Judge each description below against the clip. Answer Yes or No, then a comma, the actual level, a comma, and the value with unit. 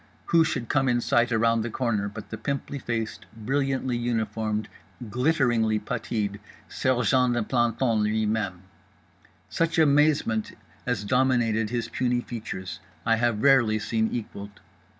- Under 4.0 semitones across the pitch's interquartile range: Yes, average, 2.8 semitones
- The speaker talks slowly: Yes, slow, 130 wpm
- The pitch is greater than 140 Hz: No, low, 115 Hz